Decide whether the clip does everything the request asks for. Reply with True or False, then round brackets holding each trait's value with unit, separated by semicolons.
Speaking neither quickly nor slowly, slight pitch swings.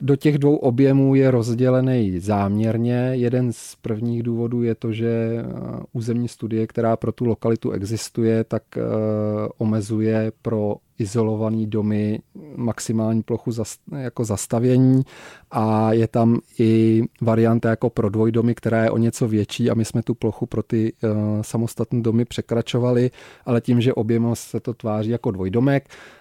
True (140 wpm; 1.6 semitones)